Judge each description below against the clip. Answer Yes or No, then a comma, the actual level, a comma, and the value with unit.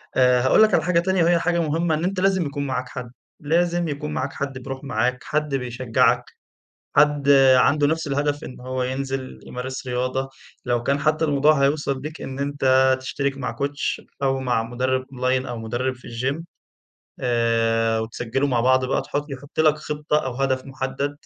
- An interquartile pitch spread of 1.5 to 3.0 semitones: Yes, average, 2.7 semitones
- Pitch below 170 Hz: Yes, low, 135 Hz